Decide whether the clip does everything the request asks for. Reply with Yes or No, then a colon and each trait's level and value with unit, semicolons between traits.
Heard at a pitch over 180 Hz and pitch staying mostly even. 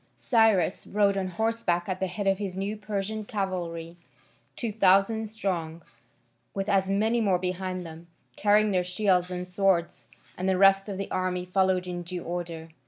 Yes: high, 190 Hz; narrow, 2.1 semitones